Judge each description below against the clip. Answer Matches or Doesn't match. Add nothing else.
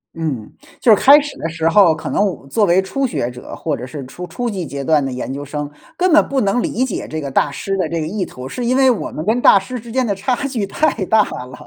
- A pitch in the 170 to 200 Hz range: Matches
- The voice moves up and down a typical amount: Doesn't match